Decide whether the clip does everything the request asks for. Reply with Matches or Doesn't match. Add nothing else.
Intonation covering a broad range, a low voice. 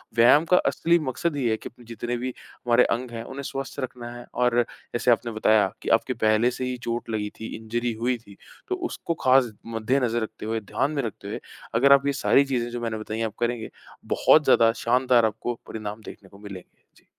Doesn't match